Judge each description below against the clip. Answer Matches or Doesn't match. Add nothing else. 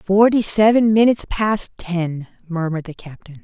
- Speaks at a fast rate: Doesn't match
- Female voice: Matches